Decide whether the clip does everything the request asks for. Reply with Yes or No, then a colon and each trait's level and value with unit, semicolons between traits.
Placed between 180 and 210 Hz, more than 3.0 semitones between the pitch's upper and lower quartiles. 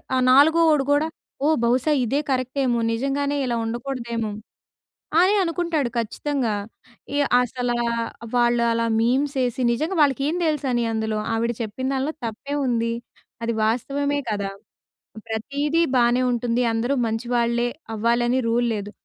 No: high, 245 Hz; average, 3.5 semitones